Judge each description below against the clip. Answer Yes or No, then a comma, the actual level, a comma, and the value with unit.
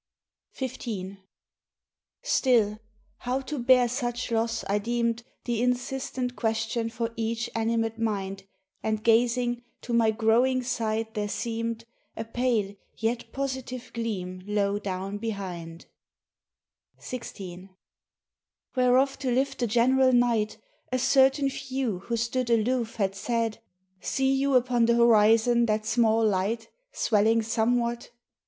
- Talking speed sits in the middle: No, slow, 120 wpm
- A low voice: No, high, 230 Hz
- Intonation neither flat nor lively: No, narrow, 2.3 semitones